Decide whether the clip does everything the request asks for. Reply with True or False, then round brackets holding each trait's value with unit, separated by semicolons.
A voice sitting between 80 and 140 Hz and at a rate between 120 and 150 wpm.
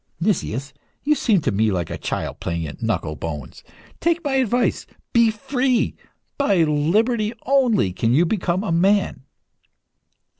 False (190 Hz; 145 wpm)